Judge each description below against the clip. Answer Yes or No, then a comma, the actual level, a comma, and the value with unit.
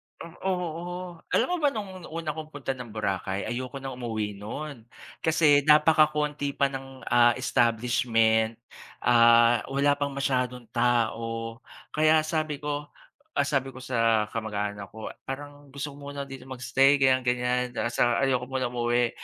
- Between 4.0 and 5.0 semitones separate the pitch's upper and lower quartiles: No, average, 3.6 semitones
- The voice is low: Yes, low, 130 Hz